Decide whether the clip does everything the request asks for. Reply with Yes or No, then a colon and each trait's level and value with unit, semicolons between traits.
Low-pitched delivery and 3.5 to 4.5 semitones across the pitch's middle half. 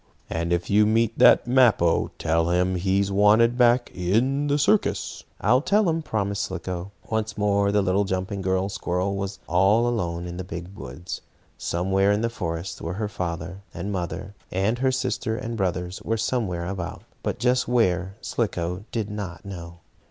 Yes: low, 100 Hz; average, 3.9 semitones